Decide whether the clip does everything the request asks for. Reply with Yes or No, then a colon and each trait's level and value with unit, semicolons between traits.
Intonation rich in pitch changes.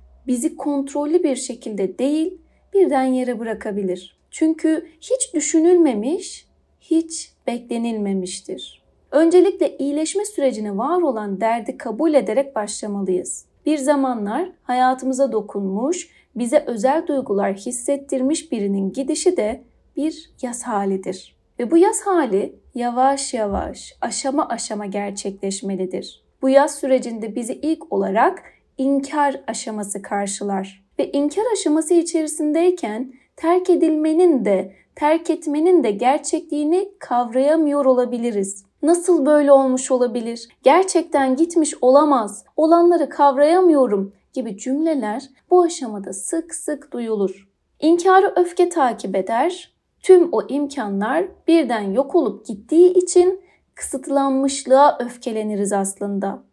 Yes: wide, 6.6 semitones